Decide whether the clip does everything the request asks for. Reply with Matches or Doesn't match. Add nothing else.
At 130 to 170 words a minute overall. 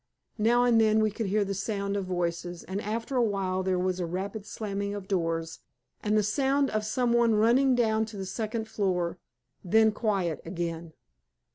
Doesn't match